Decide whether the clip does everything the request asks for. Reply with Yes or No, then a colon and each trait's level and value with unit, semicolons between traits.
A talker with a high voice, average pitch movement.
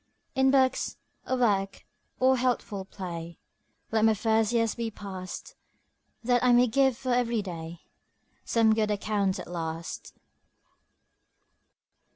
Yes: high, 220 Hz; average, 4.3 semitones